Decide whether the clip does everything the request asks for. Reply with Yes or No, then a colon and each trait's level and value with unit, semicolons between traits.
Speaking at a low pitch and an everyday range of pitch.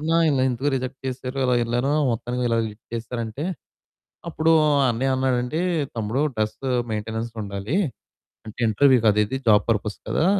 Yes: low, 120 Hz; average, 3.3 semitones